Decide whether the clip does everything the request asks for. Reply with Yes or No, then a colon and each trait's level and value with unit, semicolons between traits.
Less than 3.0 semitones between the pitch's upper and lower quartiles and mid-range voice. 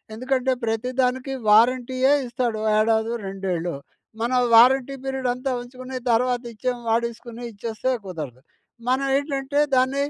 No: narrow, 2.6 semitones; very high, 250 Hz